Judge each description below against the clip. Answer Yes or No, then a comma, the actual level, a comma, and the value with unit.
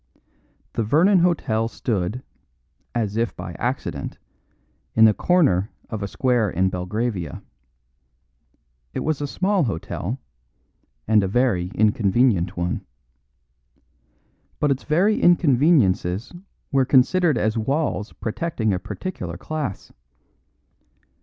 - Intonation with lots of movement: Yes, wide, 6.9 semitones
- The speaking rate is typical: No, slow, 105 wpm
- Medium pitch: No, low, 115 Hz